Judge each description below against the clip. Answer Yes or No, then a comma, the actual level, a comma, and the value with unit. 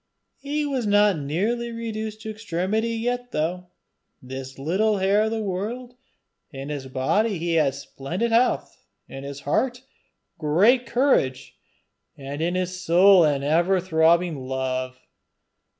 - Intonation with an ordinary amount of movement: No, wide, 7.3 semitones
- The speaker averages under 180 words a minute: Yes, slow, 135 wpm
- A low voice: No, medium, 185 Hz